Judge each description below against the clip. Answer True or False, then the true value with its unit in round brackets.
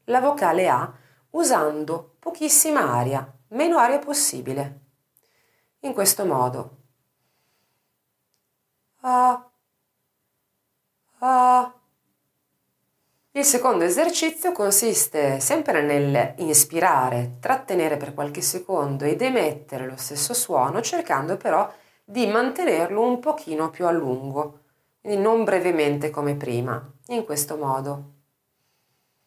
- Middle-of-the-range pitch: True (165 Hz)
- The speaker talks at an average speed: False (90 wpm)